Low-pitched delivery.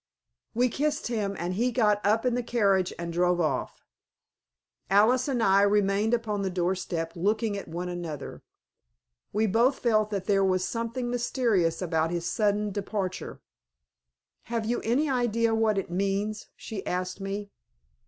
No: high, 205 Hz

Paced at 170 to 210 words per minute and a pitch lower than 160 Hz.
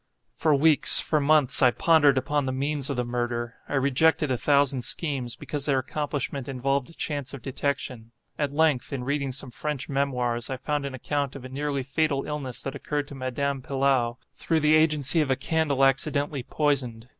Yes: average, 190 wpm; medium, 140 Hz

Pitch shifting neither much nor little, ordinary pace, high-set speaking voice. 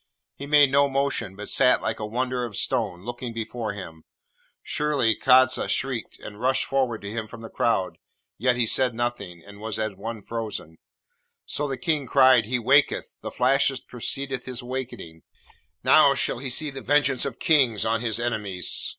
No: average, 3.4 semitones; average, 175 wpm; low, 120 Hz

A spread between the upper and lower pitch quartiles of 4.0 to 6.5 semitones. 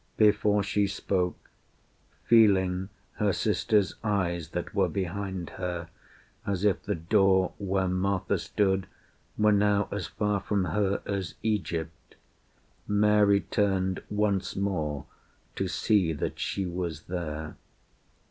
No: narrow, 2.4 semitones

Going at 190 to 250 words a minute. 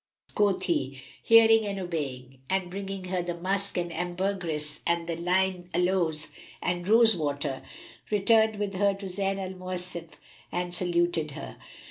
No: average, 140 wpm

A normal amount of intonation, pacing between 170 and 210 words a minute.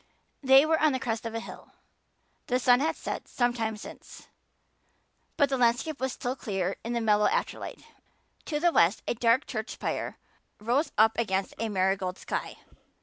Yes: average, 3.6 semitones; average, 175 wpm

